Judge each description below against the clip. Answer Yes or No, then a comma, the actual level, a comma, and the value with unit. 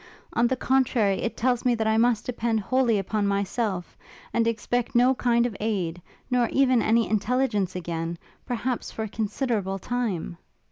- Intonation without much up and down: No, average, 3.5 semitones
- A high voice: Yes, high, 225 Hz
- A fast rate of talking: No, average, 160 wpm